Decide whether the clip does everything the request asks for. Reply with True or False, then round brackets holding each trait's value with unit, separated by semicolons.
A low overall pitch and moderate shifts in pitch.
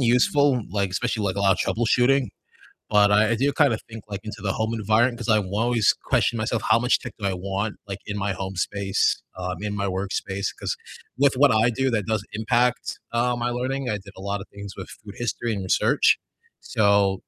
True (110 Hz; 3.3 semitones)